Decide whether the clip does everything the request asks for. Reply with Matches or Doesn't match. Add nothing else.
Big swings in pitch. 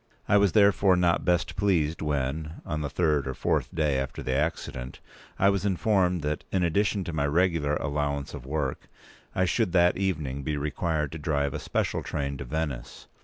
Doesn't match